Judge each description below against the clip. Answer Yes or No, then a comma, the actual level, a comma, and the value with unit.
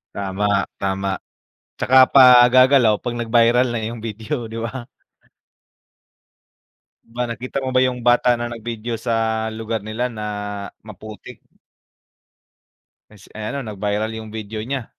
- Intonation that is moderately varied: No, narrow, 2.3 semitones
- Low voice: Yes, low, 115 Hz